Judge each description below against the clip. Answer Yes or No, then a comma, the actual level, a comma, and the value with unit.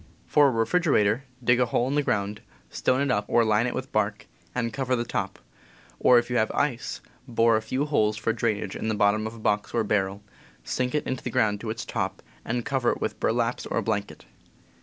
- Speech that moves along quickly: Yes, fast, 235 wpm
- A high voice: No, low, 115 Hz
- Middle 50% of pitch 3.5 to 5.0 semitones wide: No, average, 2.7 semitones